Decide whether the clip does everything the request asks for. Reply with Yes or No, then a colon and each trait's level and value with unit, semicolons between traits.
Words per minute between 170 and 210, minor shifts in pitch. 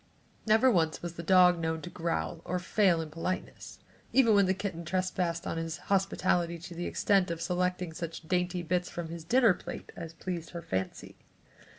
Yes: average, 185 wpm; narrow, 1.9 semitones